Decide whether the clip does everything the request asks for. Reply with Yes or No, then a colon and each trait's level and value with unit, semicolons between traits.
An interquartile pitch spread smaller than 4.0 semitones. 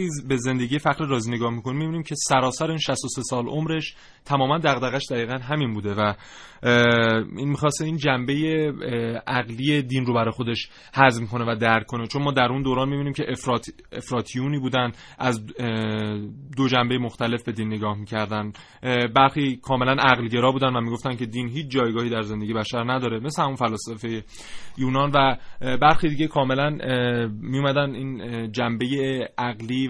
Yes: average, 2.9 semitones